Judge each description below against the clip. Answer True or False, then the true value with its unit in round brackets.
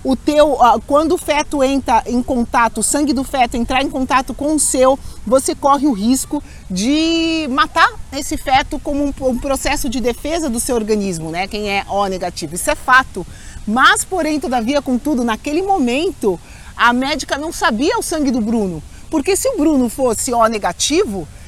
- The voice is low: False (270 Hz)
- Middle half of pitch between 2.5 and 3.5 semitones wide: False (3.9 semitones)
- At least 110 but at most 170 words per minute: False (180 wpm)